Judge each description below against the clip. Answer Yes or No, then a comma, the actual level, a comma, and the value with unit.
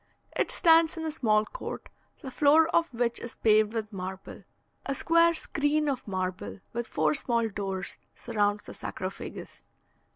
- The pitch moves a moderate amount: No, wide, 6.8 semitones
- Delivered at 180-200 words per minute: No, average, 155 wpm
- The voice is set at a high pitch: Yes, high, 235 Hz